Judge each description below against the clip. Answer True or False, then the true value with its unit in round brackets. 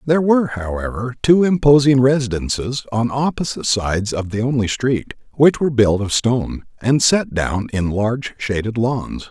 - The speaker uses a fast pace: False (160 wpm)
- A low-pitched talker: True (120 Hz)